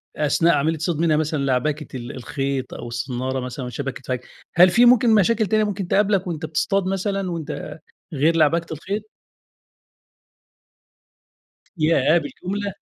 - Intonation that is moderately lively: No, wide, 5.8 semitones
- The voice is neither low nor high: Yes, medium, 160 Hz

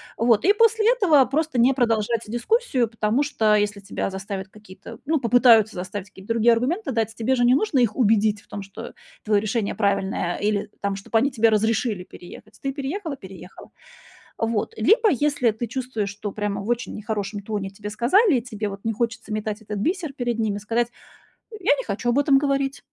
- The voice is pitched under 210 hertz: No, high, 225 Hz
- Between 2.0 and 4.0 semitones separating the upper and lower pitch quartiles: No, average, 4.4 semitones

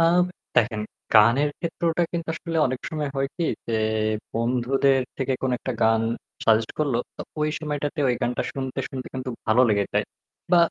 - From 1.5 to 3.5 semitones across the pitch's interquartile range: No, average, 4.1 semitones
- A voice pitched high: No, low, 130 Hz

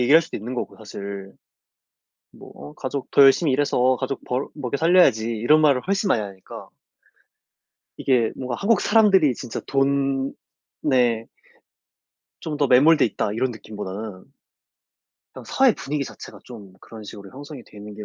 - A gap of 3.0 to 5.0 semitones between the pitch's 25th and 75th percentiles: Yes, average, 4.7 semitones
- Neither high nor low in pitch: No, low, 130 Hz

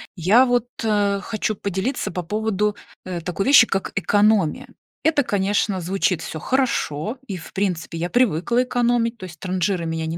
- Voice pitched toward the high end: Yes, high, 200 Hz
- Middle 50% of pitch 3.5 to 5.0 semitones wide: Yes, average, 4.2 semitones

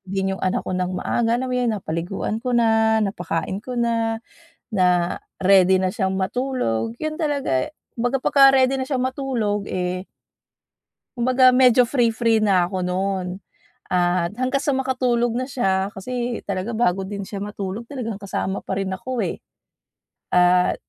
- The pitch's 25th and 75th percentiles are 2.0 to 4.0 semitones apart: No, average, 4.9 semitones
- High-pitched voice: Yes, high, 220 Hz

